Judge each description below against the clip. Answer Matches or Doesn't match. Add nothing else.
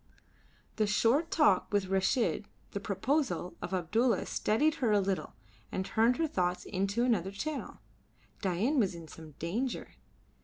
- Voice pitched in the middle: Doesn't match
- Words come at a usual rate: Matches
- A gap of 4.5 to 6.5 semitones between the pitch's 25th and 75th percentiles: Matches